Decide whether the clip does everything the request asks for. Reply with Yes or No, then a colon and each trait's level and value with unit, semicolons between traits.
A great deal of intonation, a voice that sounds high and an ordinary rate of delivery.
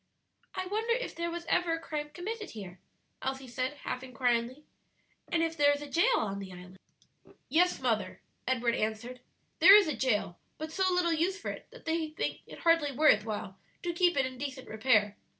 Yes: wide, 6.4 semitones; very high, 285 Hz; average, 195 wpm